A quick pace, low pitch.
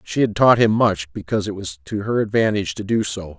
Yes: fast, 250 wpm; low, 110 Hz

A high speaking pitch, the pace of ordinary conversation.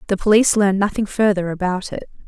Yes: high, 195 Hz; average, 185 wpm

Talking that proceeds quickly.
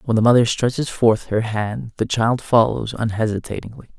No: average, 165 wpm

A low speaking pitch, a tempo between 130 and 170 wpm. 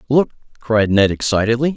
Yes: low, 120 Hz; slow, 135 wpm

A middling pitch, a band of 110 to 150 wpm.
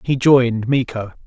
No: low, 125 Hz; average, 140 wpm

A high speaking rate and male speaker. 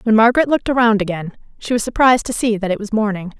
No: fast, 250 wpm; female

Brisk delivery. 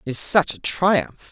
Yes: fast, 225 wpm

